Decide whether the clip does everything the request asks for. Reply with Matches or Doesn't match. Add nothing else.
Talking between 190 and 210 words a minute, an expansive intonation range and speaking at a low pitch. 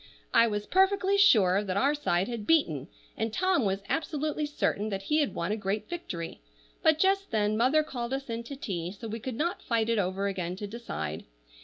Doesn't match